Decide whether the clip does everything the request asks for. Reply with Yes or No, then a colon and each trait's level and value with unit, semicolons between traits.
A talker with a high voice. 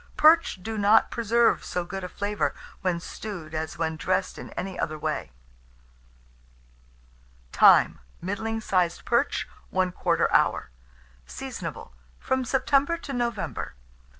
Yes: high, 195 Hz